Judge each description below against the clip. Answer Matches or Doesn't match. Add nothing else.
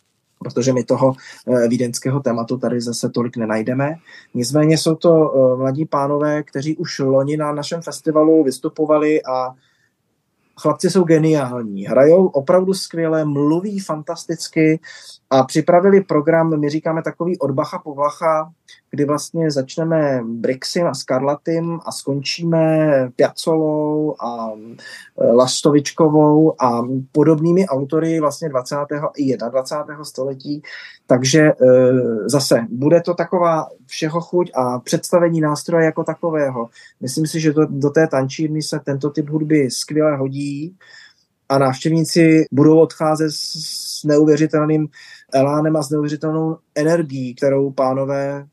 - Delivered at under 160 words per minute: Matches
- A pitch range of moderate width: Matches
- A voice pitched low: Doesn't match